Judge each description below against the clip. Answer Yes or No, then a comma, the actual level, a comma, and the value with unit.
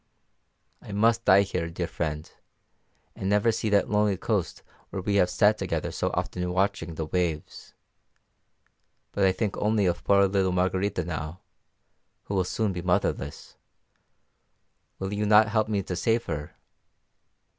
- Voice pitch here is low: Yes, very low, 95 Hz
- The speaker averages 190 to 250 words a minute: No, average, 150 wpm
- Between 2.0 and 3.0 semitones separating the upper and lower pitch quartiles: Yes, narrow, 2.6 semitones